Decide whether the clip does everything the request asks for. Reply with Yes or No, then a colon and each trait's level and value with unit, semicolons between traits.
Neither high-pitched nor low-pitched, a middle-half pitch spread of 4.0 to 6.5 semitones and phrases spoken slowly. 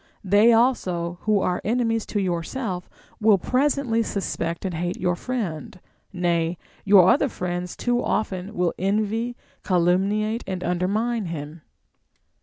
No: high, 195 Hz; average, 4.3 semitones; slow, 125 wpm